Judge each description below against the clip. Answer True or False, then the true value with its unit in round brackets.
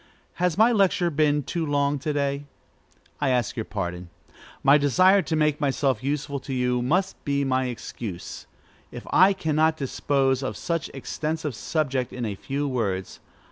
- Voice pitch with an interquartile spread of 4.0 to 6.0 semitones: False (3.5 semitones)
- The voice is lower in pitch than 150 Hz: True (140 Hz)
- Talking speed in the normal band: True (165 wpm)